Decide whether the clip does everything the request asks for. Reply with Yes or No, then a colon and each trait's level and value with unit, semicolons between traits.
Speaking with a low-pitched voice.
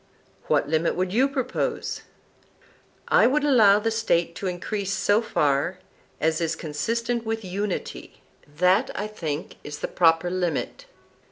No: medium, 185 Hz